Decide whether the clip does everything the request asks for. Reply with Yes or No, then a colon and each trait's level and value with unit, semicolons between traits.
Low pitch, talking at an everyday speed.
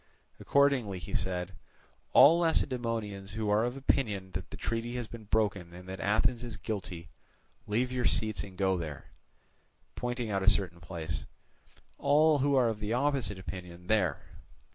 Yes: low, 105 Hz; average, 160 wpm